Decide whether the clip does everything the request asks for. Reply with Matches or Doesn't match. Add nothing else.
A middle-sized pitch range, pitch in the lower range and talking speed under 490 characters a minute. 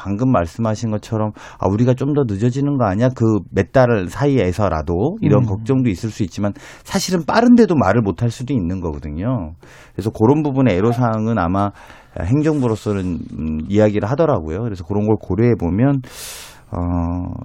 Matches